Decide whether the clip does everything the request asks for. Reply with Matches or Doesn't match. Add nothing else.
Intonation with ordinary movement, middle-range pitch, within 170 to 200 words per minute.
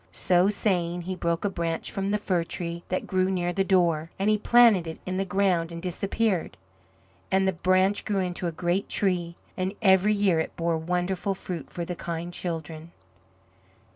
Doesn't match